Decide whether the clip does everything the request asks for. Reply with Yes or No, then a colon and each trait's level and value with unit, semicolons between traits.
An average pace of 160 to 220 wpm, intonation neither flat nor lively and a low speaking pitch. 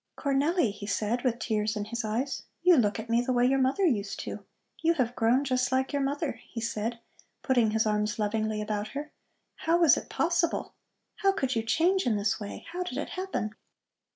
No: fast, 205 wpm; average, 4.9 semitones; high, 245 Hz